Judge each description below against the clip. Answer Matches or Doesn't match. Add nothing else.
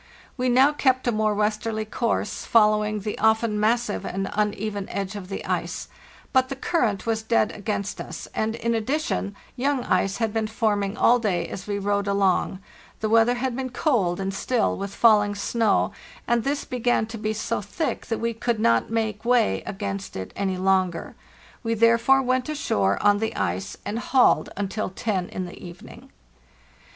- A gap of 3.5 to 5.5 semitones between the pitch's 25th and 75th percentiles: Doesn't match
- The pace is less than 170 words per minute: Doesn't match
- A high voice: Matches